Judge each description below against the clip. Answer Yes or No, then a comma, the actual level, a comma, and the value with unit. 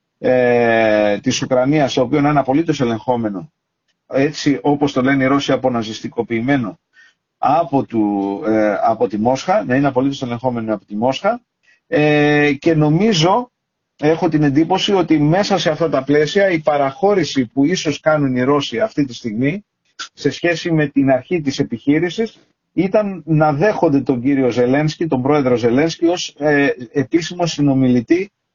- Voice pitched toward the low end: No, medium, 145 Hz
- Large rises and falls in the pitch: No, average, 4.1 semitones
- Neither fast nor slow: Yes, average, 145 wpm